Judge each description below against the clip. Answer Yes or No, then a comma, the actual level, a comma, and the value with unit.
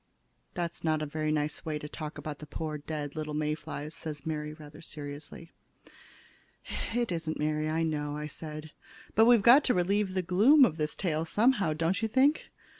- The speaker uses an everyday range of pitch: Yes, average, 3.6 semitones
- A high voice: No, medium, 155 Hz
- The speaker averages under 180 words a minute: No, average, 190 wpm